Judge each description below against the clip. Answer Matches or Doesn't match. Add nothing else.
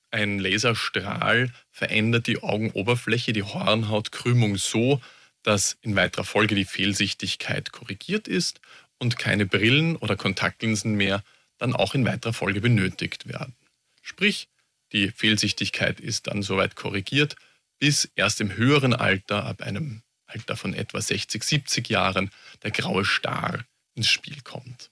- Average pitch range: Matches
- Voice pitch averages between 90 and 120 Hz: Matches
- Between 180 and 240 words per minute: Doesn't match